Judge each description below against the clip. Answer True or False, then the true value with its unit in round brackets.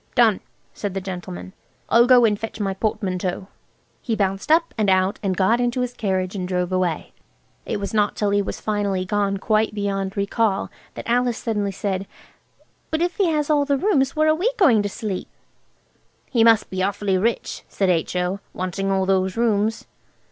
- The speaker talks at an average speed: True (175 wpm)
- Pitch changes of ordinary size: True (3.6 semitones)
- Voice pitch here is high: True (205 Hz)